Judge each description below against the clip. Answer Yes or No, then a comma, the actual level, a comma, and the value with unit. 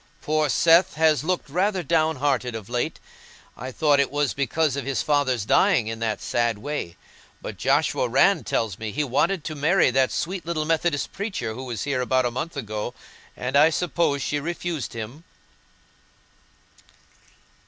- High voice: No, medium, 145 Hz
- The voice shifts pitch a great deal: No, average, 4.6 semitones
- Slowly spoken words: No, average, 165 wpm